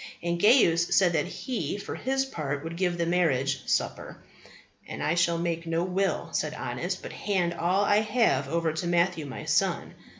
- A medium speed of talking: Yes, average, 180 wpm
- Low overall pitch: No, medium, 170 Hz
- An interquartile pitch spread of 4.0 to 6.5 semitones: No, average, 2.8 semitones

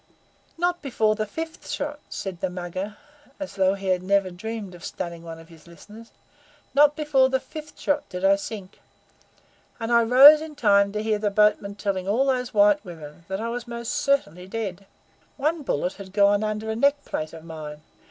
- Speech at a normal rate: Yes, average, 190 wpm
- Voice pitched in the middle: No, high, 210 Hz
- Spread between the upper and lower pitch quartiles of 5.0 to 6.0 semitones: Yes, average, 5.3 semitones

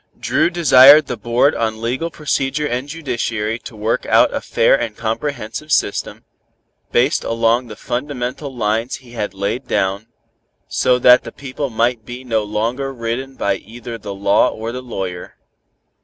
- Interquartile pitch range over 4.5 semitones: No, average, 3.2 semitones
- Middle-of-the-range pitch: No, low, 120 Hz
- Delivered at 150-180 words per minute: Yes, average, 155 wpm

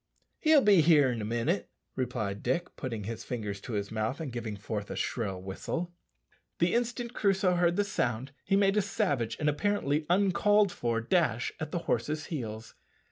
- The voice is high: No, medium, 145 Hz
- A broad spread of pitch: Yes, wide, 8.7 semitones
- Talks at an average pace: Yes, average, 180 wpm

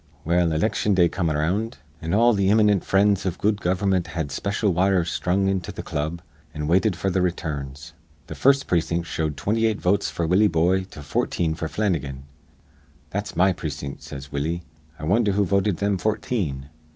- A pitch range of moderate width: Yes, average, 3.9 semitones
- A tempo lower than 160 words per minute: No, average, 175 wpm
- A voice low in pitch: Yes, very low, 90 Hz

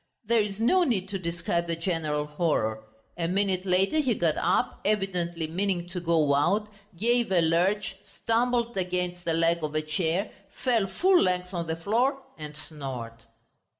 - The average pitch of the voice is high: No, medium, 180 Hz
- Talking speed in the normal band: Yes, average, 165 wpm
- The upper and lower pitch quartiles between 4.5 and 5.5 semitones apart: No, average, 3.9 semitones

